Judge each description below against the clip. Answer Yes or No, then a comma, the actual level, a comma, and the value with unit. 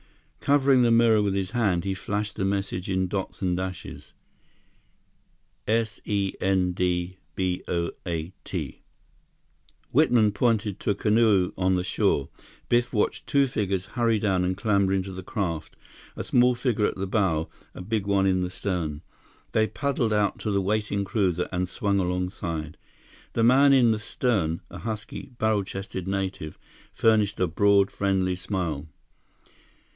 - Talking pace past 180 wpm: No, average, 155 wpm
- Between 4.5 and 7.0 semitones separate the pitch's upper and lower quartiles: No, average, 3.0 semitones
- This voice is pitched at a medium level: No, low, 100 Hz